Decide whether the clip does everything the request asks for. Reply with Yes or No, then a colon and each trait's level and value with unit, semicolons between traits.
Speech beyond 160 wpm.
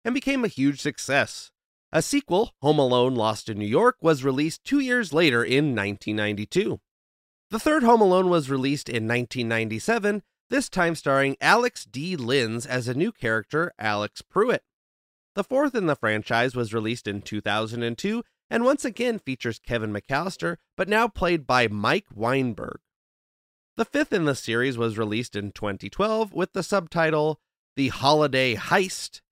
No: average, 155 wpm